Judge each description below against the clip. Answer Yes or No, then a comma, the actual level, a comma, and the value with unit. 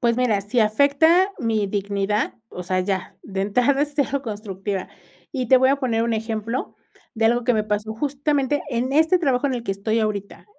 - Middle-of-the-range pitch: No, high, 230 Hz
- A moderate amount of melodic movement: Yes, average, 4.6 semitones